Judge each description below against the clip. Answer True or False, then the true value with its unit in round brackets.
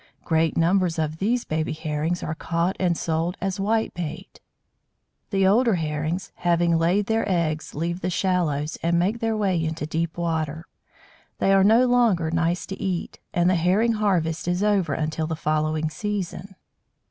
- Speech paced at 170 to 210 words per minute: False (160 wpm)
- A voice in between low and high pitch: True (175 Hz)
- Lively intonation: False (3.3 semitones)